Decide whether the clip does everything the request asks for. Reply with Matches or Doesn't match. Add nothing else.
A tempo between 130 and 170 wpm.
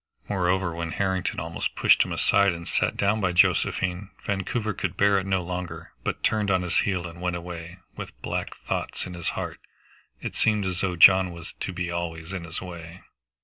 Doesn't match